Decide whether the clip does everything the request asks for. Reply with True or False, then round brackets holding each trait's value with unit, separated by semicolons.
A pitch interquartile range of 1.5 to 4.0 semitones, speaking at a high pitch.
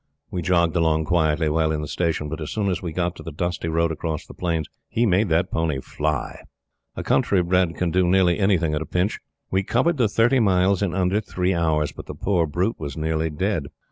False (2.9 semitones; 85 Hz)